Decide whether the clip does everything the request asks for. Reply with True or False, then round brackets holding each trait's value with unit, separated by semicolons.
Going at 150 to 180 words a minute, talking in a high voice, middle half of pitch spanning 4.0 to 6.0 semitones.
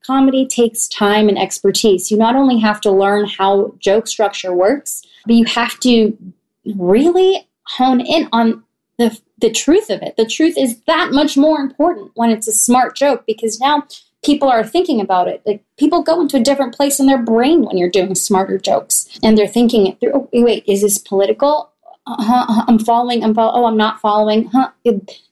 False (200 wpm; 230 Hz; 4.6 semitones)